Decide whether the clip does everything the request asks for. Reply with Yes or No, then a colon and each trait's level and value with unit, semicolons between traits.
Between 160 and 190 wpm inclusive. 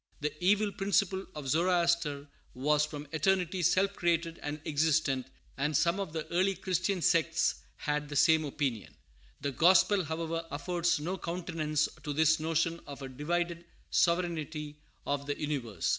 No: average, 145 wpm